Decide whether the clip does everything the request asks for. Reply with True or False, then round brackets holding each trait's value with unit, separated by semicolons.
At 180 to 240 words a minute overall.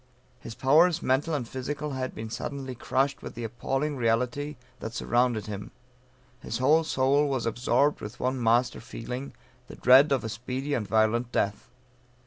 False (160 wpm)